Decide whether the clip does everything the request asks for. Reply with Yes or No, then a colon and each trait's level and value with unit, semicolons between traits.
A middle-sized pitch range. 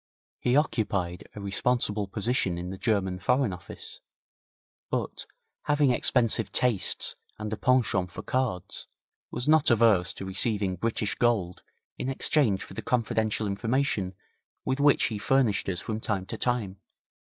Yes: average, 4.5 semitones